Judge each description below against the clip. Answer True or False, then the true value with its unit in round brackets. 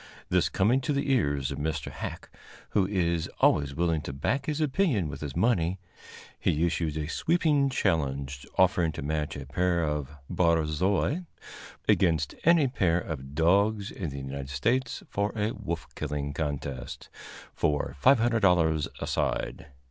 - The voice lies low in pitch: True (85 Hz)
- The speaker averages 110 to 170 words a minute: True (150 wpm)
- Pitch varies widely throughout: True (6.5 semitones)